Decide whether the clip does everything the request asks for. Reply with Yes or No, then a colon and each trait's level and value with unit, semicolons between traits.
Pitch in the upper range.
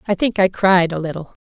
No: medium, 180 Hz